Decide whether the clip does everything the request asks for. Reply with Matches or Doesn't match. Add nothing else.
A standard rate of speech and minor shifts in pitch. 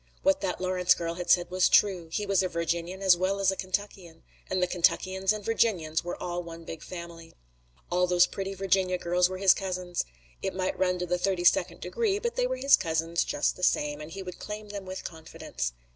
Doesn't match